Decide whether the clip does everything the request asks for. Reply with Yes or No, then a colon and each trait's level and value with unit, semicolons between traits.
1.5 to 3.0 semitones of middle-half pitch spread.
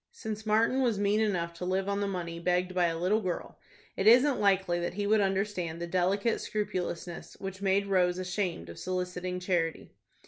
Yes: narrow, 2.4 semitones